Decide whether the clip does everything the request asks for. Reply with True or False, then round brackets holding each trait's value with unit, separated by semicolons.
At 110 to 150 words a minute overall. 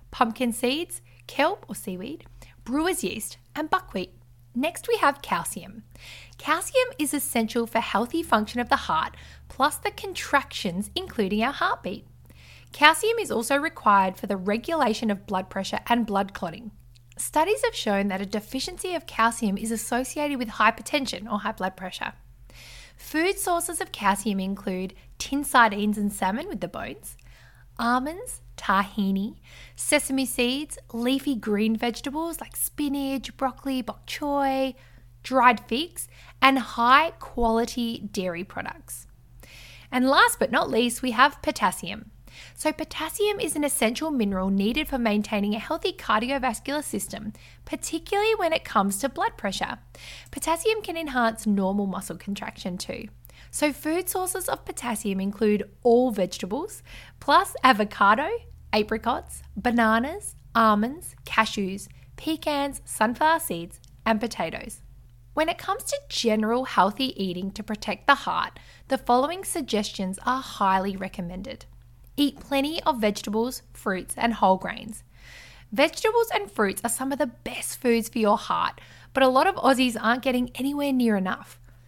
True (140 wpm)